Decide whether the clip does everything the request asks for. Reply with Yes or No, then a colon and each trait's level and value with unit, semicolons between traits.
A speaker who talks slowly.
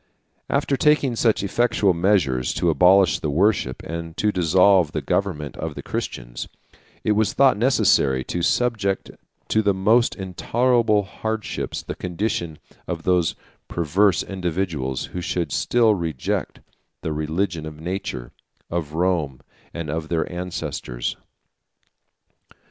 Yes: slow, 125 wpm